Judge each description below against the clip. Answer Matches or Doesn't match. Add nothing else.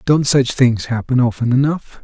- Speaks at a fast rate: Doesn't match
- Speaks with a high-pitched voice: Doesn't match